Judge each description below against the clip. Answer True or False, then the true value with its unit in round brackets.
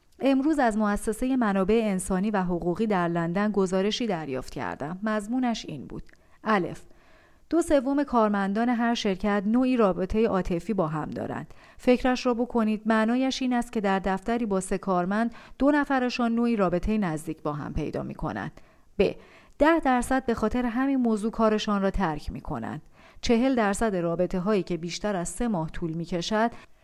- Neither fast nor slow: False (165 wpm)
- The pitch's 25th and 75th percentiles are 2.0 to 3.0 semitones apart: False (4.3 semitones)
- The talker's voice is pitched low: False (215 Hz)